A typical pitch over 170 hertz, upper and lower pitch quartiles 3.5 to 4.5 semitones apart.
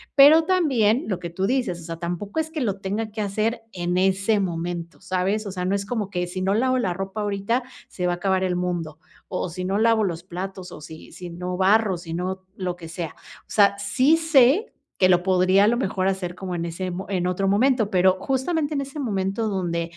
Yes: high, 190 Hz; average, 3.8 semitones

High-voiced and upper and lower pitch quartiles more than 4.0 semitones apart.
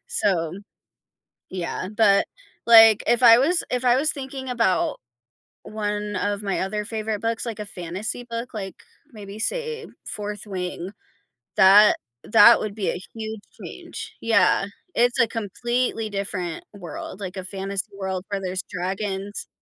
No: high, 210 Hz; average, 3.0 semitones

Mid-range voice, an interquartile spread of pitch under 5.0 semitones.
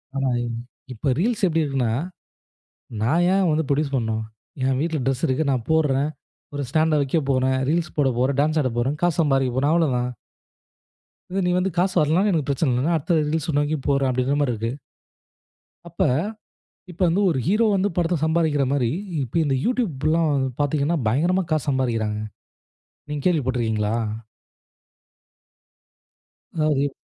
Yes: medium, 145 Hz; average, 3.9 semitones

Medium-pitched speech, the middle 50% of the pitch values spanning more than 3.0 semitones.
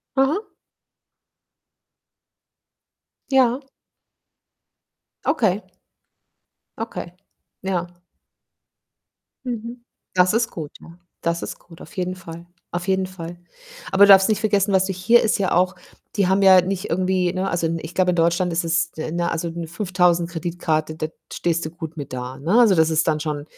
No: medium, 180 Hz; average, 2.7 semitones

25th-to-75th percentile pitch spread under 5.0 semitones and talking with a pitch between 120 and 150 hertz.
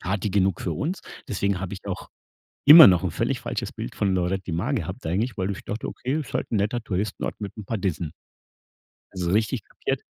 No: average, 2.8 semitones; low, 100 Hz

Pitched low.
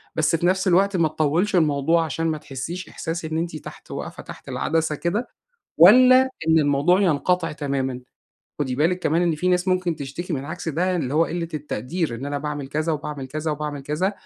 No: medium, 160 Hz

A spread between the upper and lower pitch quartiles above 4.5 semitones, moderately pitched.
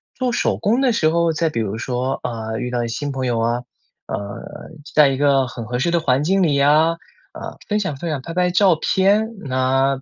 Yes: average, 5.2 semitones; medium, 145 Hz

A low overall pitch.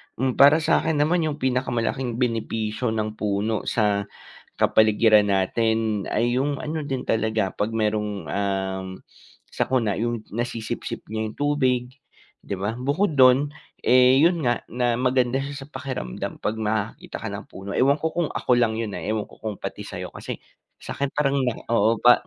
Yes: low, 120 Hz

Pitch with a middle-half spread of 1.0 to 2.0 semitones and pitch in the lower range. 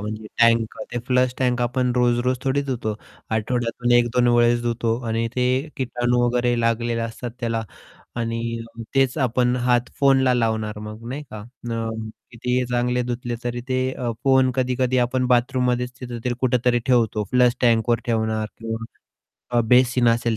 Yes: narrow, 1.4 semitones; low, 120 Hz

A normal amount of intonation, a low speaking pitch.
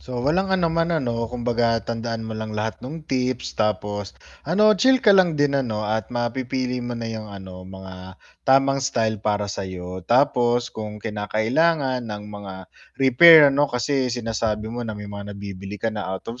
Yes: average, 4.1 semitones; low, 115 Hz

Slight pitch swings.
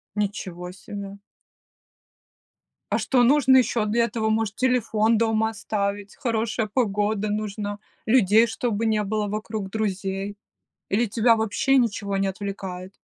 Yes: narrow, 2.2 semitones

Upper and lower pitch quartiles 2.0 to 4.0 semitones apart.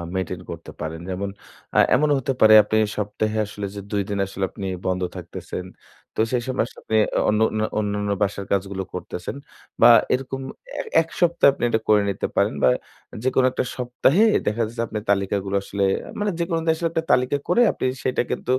No: average, 4.6 semitones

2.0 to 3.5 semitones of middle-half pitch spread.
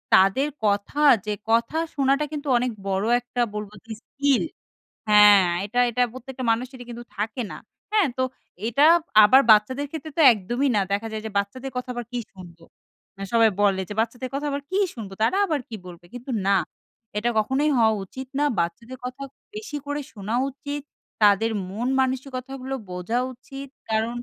No: average, 4.4 semitones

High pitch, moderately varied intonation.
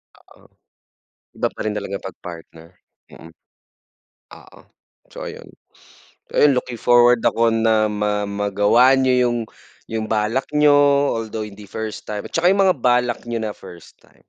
No: low, 110 Hz; average, 3.3 semitones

